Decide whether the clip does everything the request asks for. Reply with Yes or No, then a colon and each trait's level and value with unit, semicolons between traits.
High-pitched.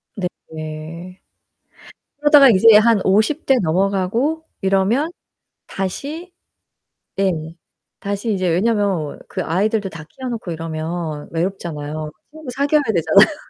Yes: high, 195 Hz